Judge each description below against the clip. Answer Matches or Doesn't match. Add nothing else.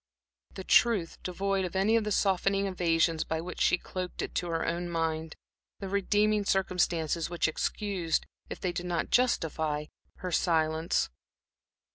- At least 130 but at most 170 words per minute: Matches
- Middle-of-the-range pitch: Matches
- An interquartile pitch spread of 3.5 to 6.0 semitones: Doesn't match